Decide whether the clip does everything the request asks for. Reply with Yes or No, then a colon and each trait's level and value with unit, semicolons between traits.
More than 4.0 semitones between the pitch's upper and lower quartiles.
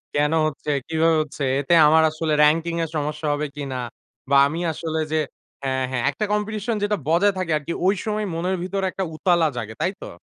No: average, 3.7 semitones